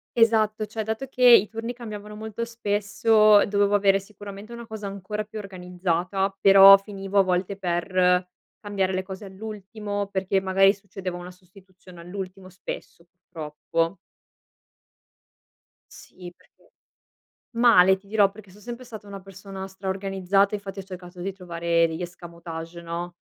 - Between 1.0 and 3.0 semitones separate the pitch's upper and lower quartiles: Yes, narrow, 2.4 semitones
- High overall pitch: Yes, high, 195 Hz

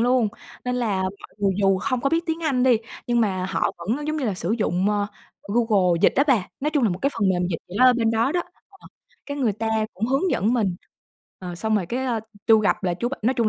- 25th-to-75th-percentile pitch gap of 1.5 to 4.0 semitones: No, average, 4.9 semitones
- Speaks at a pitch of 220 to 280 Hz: Yes, high, 225 Hz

